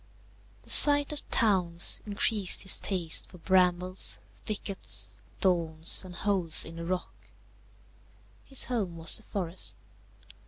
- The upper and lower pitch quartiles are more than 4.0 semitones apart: No, average, 3.2 semitones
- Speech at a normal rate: No, slow, 120 wpm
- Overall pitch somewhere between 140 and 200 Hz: Yes, medium, 185 Hz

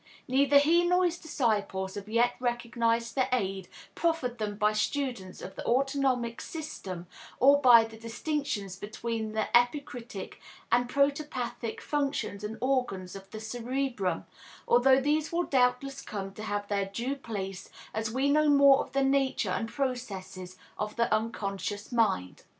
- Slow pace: No, average, 150 wpm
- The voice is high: Yes, high, 240 Hz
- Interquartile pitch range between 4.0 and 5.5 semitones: Yes, average, 4.7 semitones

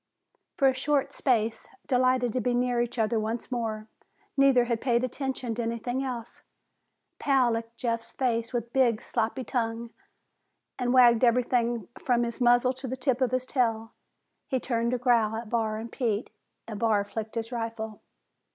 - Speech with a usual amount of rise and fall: No, narrow, 1.9 semitones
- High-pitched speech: Yes, high, 240 Hz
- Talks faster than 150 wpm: Yes, average, 170 wpm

